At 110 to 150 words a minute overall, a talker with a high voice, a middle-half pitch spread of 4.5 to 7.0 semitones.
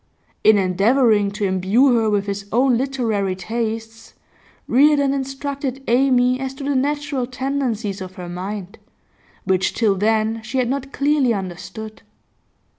Yes: slow, 135 wpm; high, 230 Hz; average, 4.8 semitones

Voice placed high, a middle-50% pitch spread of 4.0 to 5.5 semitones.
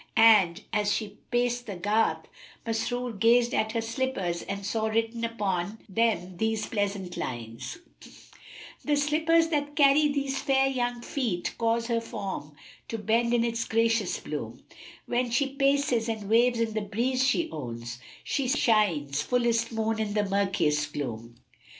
No: high, 225 Hz; average, 3.6 semitones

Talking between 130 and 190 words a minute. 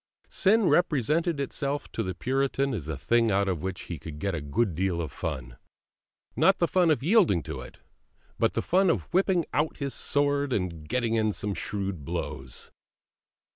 Yes: average, 180 wpm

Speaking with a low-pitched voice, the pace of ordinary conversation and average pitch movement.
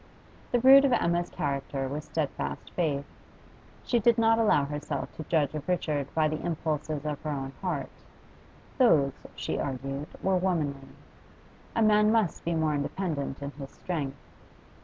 No: medium, 155 Hz; average, 155 wpm; average, 4.7 semitones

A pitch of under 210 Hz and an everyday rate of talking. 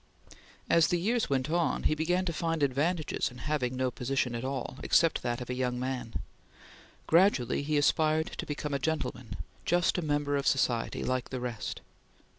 Yes: medium, 140 Hz; average, 175 wpm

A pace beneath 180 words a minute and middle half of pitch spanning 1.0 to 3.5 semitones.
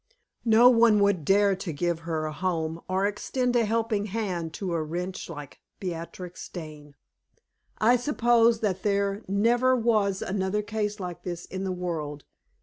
No: average, 155 wpm; average, 4.1 semitones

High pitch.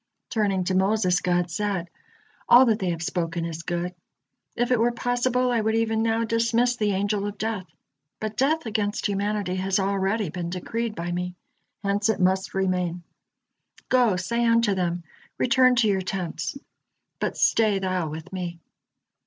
Yes: high, 200 Hz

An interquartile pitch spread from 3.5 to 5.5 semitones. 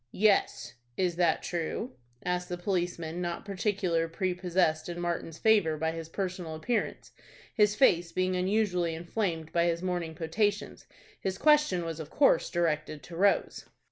No: average, 2.7 semitones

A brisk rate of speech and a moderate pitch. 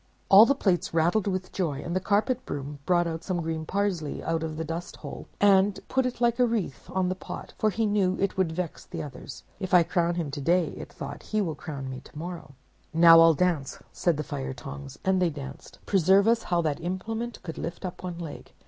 Yes: fast, 225 wpm; medium, 175 Hz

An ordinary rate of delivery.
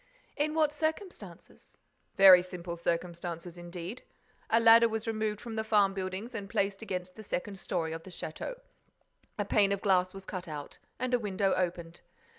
Yes: average, 170 wpm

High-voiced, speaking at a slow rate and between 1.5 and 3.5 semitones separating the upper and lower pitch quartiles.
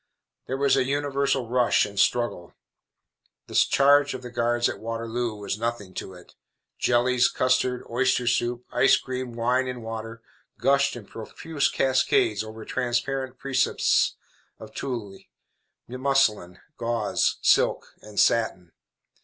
No: low, 120 Hz; slow, 130 wpm; narrow, 2.6 semitones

